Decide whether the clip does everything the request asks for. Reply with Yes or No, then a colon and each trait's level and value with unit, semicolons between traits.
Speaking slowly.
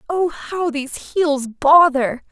Yes: slow, 130 wpm